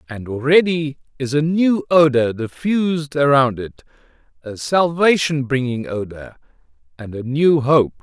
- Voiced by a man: Yes, male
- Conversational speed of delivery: No, slow, 120 wpm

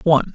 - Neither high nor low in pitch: Yes, medium, 155 Hz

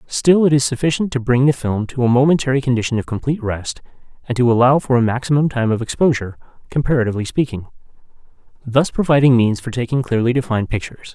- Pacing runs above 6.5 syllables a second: Yes, 6.8 syllables/s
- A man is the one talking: Yes, male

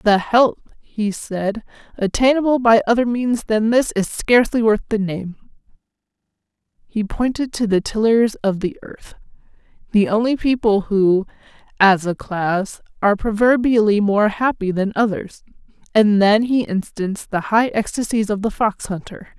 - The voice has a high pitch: Yes, high, 215 Hz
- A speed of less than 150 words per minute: Yes, average, 140 wpm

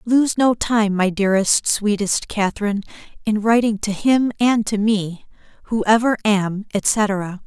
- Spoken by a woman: Yes, female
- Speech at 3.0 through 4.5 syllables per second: Yes, 4.2 syllables/s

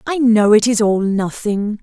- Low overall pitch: No, high, 220 Hz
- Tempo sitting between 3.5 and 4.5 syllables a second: Yes, 4.2 syllables/s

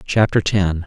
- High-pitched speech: No, very low, 95 Hz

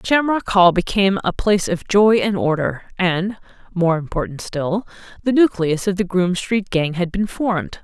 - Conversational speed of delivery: Yes, average, 160 wpm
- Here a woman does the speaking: Yes, female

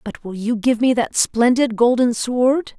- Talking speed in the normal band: Yes, average, 195 wpm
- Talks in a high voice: Yes, high, 240 Hz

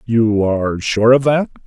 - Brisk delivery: No, average, 180 wpm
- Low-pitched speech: Yes, low, 115 Hz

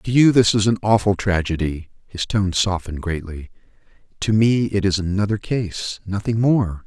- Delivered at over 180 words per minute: No, average, 165 wpm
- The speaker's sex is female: No, male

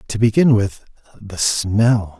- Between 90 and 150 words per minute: Yes, slow, 135 wpm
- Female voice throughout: No, male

